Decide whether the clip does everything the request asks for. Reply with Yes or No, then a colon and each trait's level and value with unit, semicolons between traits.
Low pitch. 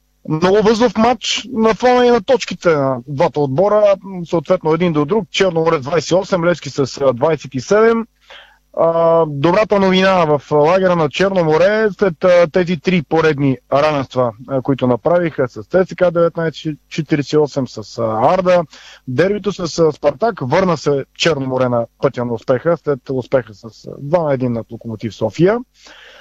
No: medium, 165 Hz